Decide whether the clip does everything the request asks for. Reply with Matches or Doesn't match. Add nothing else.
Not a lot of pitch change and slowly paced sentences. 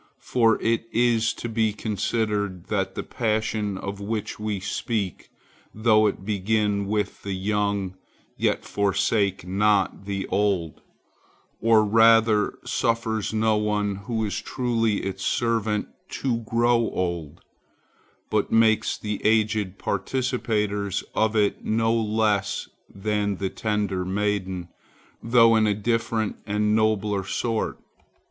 Matches